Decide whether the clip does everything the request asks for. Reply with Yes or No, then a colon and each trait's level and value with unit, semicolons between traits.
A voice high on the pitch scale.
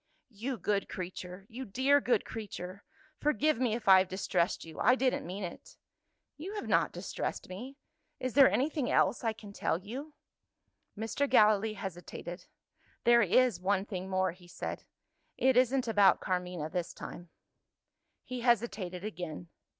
Yes: high, 210 Hz